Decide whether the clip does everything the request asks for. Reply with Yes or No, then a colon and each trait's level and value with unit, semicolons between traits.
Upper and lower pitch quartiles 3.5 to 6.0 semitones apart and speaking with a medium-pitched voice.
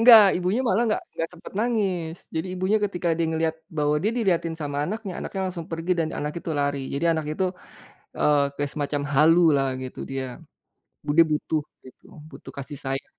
Yes: average, 4.2 semitones; medium, 165 Hz